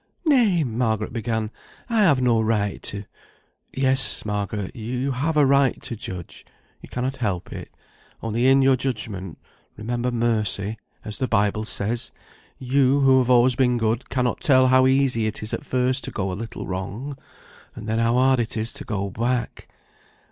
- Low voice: Yes, low, 120 Hz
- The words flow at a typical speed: Yes, average, 175 wpm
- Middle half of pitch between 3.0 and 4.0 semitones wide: Yes, average, 3.4 semitones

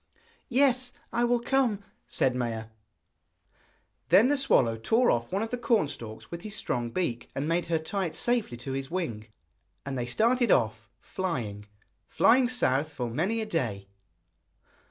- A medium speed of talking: Yes, average, 160 wpm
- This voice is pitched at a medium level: Yes, medium, 165 Hz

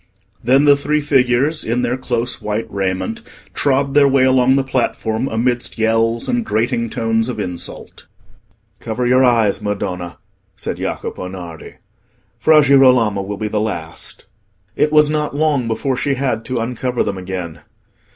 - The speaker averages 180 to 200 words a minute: No, average, 150 wpm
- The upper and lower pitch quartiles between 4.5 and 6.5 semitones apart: No, average, 4.0 semitones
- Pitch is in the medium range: No, low, 120 Hz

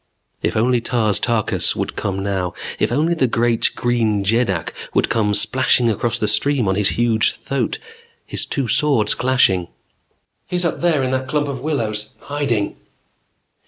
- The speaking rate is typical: Yes, average, 160 wpm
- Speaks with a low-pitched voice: Yes, low, 120 Hz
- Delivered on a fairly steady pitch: No, average, 4.1 semitones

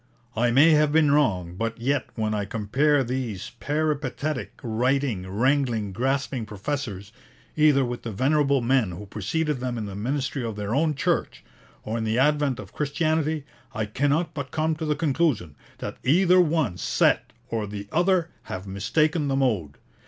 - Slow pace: No, average, 165 wpm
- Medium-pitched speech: No, low, 130 Hz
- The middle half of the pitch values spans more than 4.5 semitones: Yes, wide, 5.6 semitones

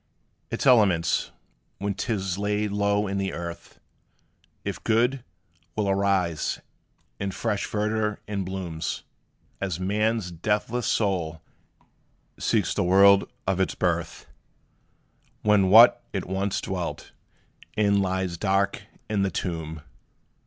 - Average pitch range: No, narrow, 2.2 semitones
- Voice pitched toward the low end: Yes, low, 100 Hz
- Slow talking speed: Yes, slow, 115 wpm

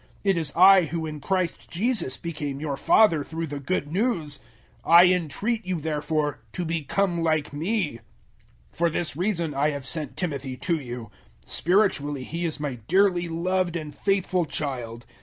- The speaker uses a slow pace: No, average, 165 wpm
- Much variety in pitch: No, average, 3.9 semitones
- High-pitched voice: No, medium, 165 Hz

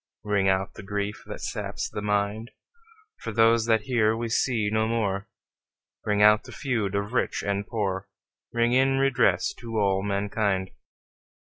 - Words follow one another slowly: No, average, 155 wpm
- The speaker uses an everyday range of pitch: No, narrow, 2.3 semitones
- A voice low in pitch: Yes, low, 105 Hz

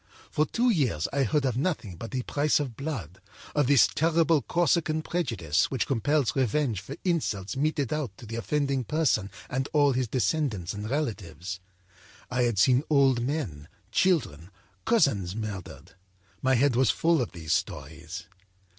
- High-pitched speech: No, low, 130 Hz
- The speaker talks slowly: No, average, 155 wpm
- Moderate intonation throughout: No, wide, 6.3 semitones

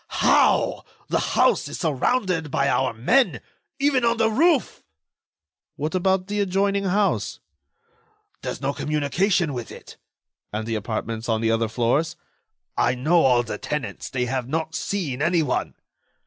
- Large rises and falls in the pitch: Yes, wide, 7.9 semitones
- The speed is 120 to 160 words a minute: Yes, average, 140 wpm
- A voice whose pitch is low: No, medium, 155 Hz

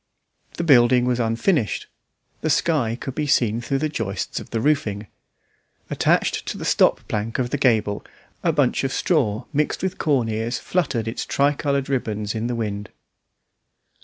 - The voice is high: No, low, 120 Hz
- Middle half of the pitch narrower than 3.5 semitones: No, average, 4.3 semitones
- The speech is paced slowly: No, average, 160 wpm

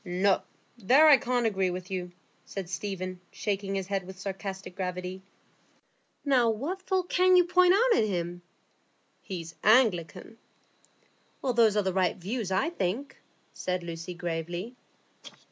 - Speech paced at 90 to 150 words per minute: Yes, average, 145 wpm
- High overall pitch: Yes, high, 195 Hz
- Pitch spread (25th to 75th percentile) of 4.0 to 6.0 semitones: Yes, average, 5.1 semitones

